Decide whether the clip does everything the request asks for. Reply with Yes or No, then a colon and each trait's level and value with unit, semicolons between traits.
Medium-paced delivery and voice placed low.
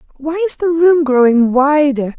No: average, 165 wpm; very high, 290 Hz